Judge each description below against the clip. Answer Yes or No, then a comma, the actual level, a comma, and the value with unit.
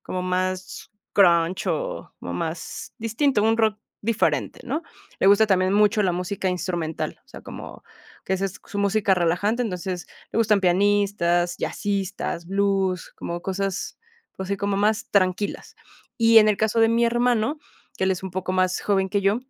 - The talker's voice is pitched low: No, high, 195 Hz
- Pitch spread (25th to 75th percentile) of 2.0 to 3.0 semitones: Yes, narrow, 2.6 semitones